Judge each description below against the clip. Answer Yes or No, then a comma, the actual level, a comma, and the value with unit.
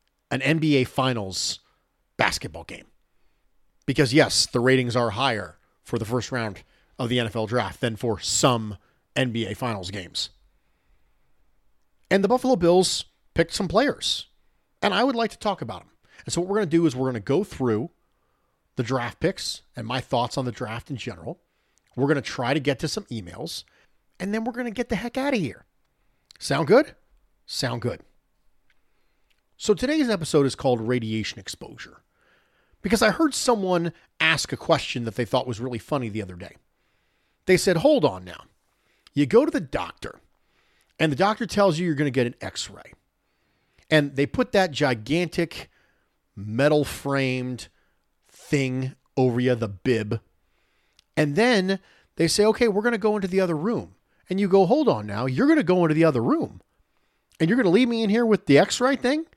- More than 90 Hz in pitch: Yes, medium, 140 Hz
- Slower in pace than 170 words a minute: No, average, 185 wpm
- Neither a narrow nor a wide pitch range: No, wide, 8.6 semitones